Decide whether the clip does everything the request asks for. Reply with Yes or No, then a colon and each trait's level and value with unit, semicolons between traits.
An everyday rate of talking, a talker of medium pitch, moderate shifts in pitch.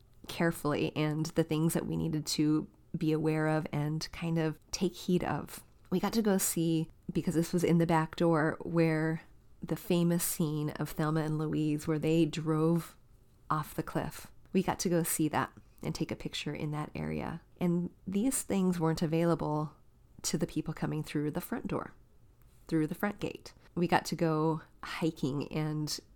No: average, 180 wpm; medium, 160 Hz; narrow, 1.9 semitones